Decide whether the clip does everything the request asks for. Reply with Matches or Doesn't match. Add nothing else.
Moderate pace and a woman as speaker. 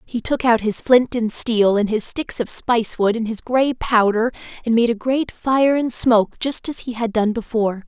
Doesn't match